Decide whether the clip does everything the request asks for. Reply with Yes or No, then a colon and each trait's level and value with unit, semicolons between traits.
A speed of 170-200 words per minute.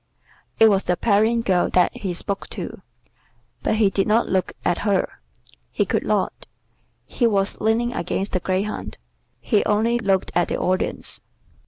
No: average, 160 wpm